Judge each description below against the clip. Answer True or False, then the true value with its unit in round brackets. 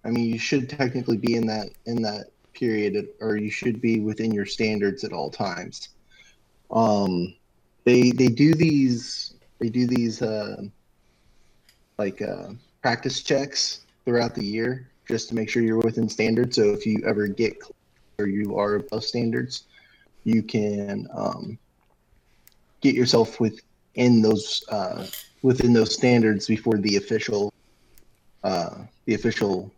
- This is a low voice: True (115 Hz)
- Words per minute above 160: False (145 wpm)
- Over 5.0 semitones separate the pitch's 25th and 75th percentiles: False (2.6 semitones)